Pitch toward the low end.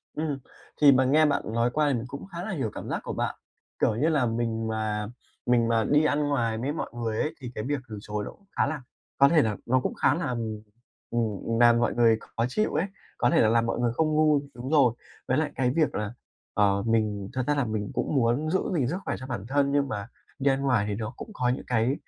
Yes: low, 125 Hz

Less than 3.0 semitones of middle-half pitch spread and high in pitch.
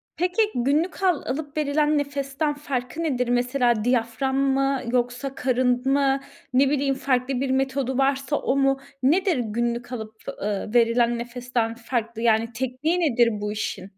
Yes: narrow, 2.6 semitones; very high, 260 Hz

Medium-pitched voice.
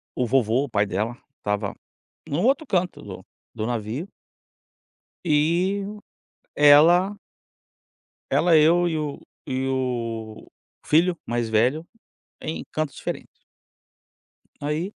Yes: medium, 145 Hz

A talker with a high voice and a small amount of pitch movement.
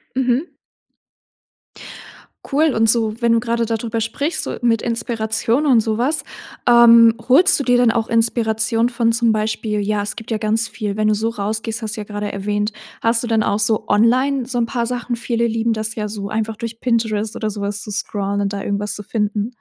Yes: high, 225 Hz; narrow, 1.8 semitones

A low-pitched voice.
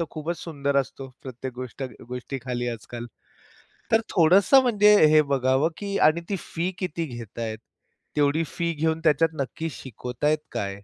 No: medium, 145 Hz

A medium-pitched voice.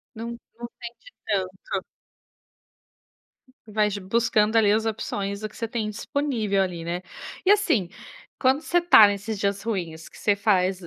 No: high, 210 Hz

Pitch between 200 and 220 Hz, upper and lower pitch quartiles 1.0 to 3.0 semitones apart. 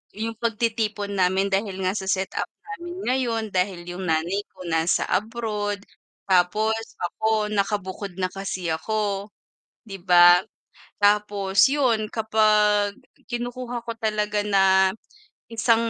Yes: high, 205 Hz; narrow, 2.6 semitones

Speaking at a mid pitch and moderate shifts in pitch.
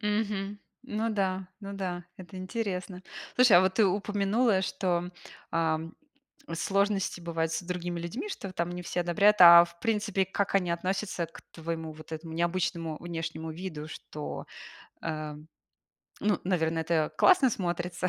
Yes: medium, 180 Hz; average, 3.0 semitones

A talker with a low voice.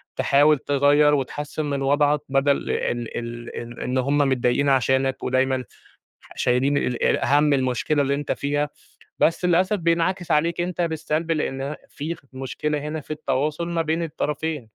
No: medium, 145 Hz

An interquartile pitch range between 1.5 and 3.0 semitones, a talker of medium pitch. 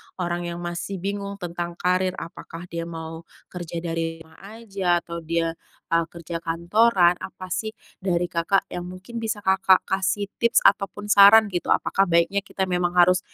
Yes: narrow, 2.5 semitones; medium, 180 Hz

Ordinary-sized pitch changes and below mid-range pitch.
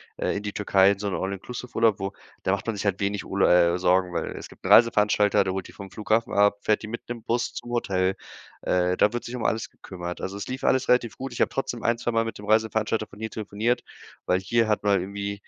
Yes: average, 3.0 semitones; low, 105 Hz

